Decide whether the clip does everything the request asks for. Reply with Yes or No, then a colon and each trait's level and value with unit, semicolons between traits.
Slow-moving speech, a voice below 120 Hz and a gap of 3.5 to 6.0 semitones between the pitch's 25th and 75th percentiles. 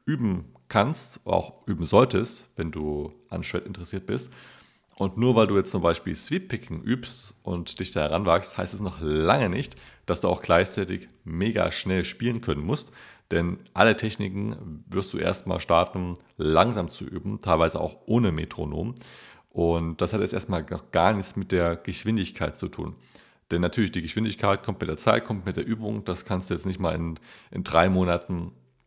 No: average, 180 wpm; very low, 90 Hz; average, 3.8 semitones